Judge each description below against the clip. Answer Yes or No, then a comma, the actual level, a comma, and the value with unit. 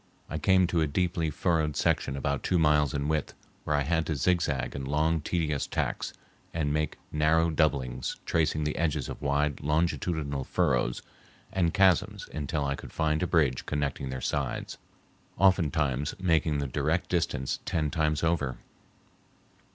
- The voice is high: No, very low, 75 Hz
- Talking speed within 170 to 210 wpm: No, average, 155 wpm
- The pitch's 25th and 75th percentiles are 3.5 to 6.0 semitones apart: No, average, 2.7 semitones